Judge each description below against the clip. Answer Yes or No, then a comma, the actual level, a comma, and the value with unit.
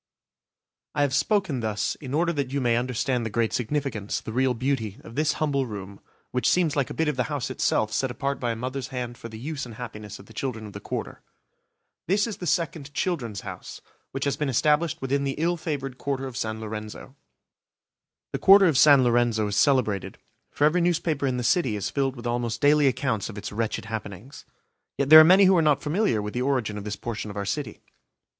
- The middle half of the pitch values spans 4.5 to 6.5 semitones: Yes, average, 4.8 semitones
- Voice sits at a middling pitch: No, low, 130 Hz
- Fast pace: Yes, fast, 220 wpm